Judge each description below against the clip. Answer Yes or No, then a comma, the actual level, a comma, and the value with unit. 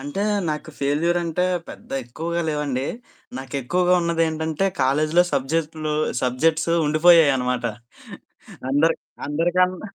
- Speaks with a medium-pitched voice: Yes, medium, 155 Hz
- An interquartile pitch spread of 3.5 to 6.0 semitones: No, average, 3.0 semitones